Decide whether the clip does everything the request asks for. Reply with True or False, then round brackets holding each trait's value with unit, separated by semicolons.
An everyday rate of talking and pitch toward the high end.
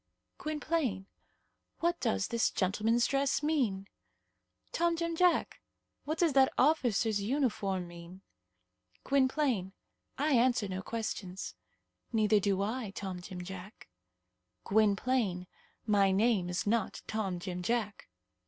False (115 wpm; 215 Hz)